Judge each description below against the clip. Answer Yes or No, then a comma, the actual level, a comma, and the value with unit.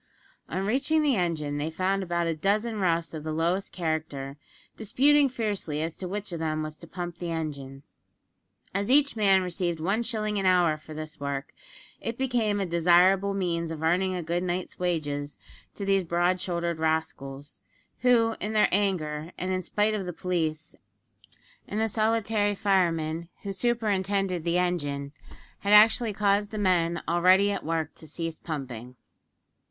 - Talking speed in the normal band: Yes, average, 165 wpm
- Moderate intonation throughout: Yes, average, 4.1 semitones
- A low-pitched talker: No, medium, 180 Hz